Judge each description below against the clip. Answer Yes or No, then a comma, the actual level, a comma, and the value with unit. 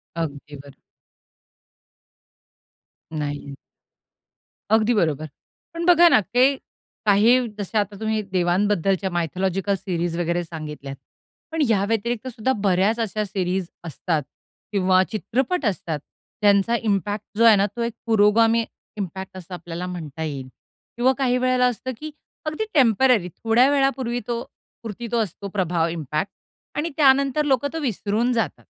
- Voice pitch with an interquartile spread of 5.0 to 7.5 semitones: Yes, wide, 5.4 semitones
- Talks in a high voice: Yes, high, 205 Hz